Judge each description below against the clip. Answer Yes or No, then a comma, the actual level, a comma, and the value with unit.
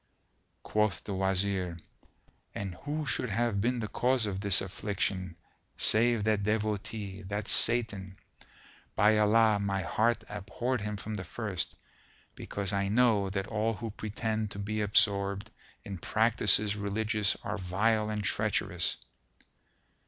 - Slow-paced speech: Yes, slow, 130 wpm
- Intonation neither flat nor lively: No, narrow, 1.9 semitones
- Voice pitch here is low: Yes, low, 105 Hz